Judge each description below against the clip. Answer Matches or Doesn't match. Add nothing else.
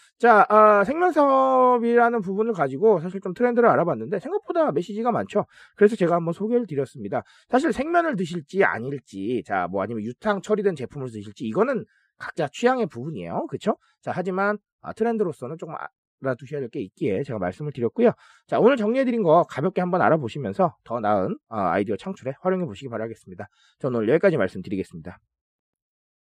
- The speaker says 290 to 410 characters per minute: Doesn't match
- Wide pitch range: Matches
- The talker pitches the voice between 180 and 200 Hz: Matches